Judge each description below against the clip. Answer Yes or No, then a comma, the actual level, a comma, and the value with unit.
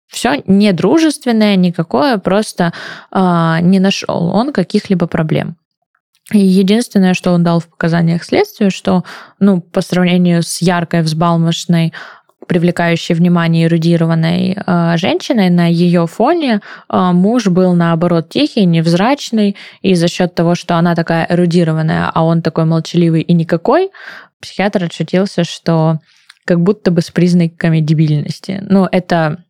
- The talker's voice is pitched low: No, medium, 175 Hz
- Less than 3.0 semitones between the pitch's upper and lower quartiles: Yes, narrow, 2.6 semitones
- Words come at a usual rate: Yes, average, 130 wpm